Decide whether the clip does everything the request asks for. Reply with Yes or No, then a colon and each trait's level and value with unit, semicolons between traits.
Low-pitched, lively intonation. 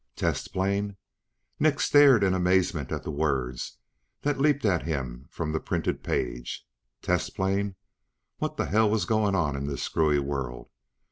Yes: very low, 90 Hz; wide, 6.3 semitones